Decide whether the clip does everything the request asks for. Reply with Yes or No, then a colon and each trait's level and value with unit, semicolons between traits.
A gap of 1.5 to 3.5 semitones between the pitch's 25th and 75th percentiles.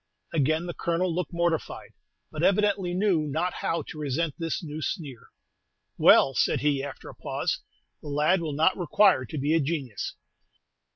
Yes: average, 3.1 semitones